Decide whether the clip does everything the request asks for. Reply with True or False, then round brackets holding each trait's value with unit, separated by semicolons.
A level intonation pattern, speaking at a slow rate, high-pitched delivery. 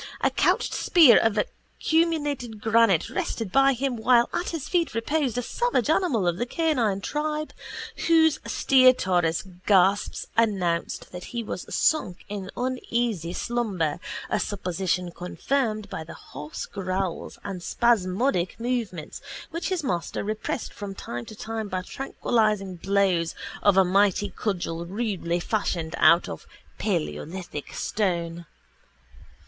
False (5.5 semitones; 125 wpm; 205 Hz)